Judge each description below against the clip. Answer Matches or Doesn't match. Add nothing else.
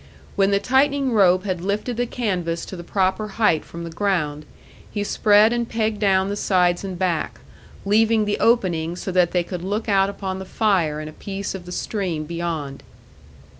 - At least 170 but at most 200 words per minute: Matches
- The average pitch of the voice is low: Doesn't match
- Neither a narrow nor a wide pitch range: Matches